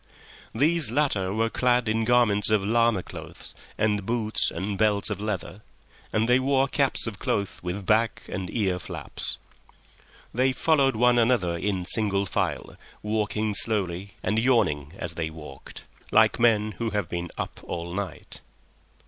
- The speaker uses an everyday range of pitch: Yes, average, 3.7 semitones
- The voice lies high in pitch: No, low, 105 Hz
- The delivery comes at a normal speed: Yes, average, 150 wpm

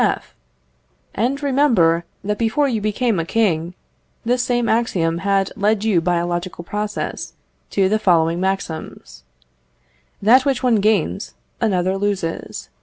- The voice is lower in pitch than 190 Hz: No, high, 200 Hz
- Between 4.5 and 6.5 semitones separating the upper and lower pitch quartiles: Yes, average, 4.8 semitones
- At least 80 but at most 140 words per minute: Yes, slow, 135 wpm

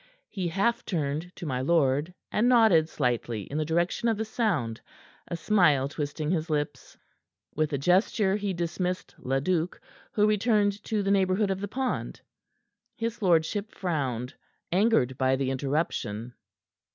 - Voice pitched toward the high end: No, medium, 170 Hz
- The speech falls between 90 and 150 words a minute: Yes, average, 145 wpm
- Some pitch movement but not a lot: No, wide, 6.3 semitones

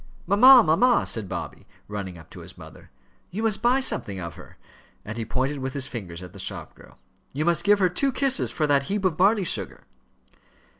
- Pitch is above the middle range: No, medium, 155 Hz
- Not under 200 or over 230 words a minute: Yes, fast, 205 wpm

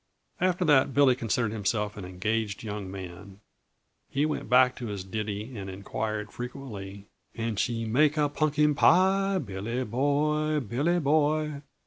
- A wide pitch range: Yes, wide, 6.3 semitones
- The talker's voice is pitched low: Yes, low, 120 Hz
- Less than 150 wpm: Yes, average, 140 wpm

